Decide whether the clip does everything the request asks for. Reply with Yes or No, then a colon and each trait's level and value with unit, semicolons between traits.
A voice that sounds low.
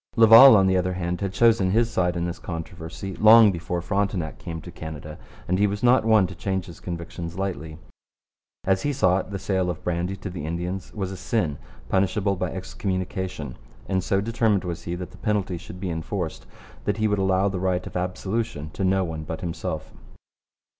Yes: very low, 95 Hz